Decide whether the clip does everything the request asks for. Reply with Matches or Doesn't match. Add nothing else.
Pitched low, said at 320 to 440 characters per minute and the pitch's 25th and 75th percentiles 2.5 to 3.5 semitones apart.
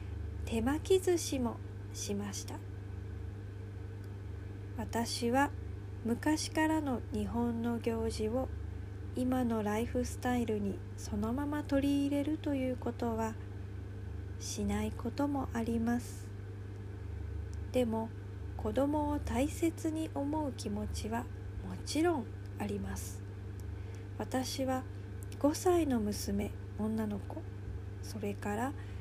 Doesn't match